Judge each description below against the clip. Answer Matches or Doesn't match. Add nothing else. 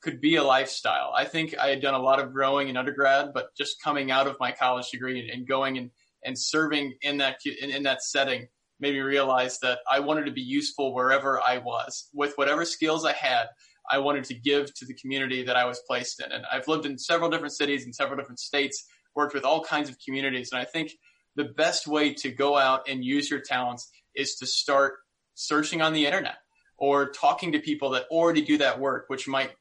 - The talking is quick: Matches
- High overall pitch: Doesn't match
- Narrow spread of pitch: Matches